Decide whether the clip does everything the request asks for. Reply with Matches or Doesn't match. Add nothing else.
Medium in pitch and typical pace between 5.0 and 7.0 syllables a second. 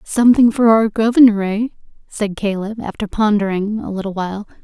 Doesn't match